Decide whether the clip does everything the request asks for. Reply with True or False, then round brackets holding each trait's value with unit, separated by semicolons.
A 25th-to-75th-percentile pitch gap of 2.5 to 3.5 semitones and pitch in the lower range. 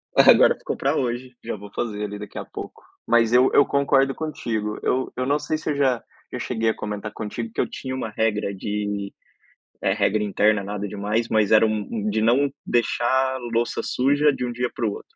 False (3.9 semitones; 115 Hz)